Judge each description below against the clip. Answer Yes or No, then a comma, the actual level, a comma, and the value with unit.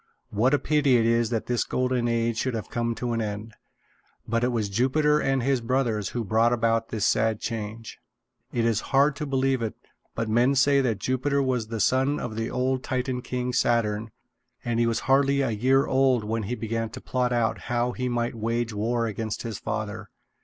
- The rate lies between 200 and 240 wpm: Yes, fast, 205 wpm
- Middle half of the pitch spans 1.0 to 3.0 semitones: Yes, narrow, 2.4 semitones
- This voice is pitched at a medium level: No, low, 120 Hz